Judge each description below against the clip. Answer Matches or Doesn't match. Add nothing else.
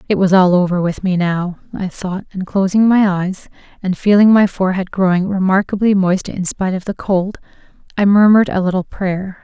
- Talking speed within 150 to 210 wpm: Matches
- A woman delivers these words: Matches